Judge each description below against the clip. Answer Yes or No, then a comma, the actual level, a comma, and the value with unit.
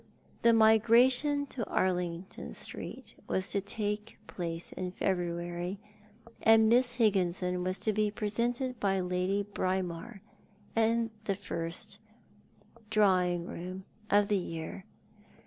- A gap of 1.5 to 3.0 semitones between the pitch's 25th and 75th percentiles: No, average, 3.5 semitones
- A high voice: Yes, high, 200 Hz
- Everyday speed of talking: No, slow, 115 wpm